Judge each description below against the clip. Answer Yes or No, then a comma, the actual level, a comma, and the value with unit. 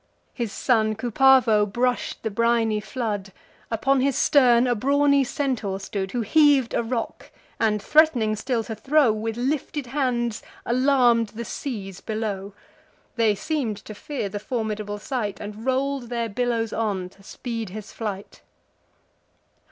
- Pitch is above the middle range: Yes, high, 230 Hz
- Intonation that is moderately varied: Yes, average, 3.4 semitones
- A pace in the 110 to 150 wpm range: Yes, average, 140 wpm